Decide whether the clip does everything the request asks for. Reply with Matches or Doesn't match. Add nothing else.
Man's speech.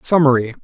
Matches